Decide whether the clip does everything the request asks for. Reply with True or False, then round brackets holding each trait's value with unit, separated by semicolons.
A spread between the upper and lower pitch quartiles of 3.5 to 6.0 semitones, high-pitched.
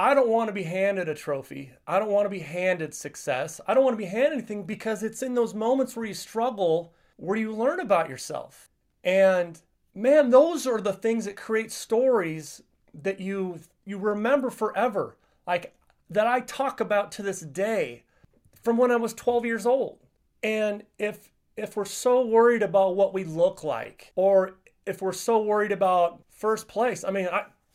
True (3.8 semitones; 210 Hz)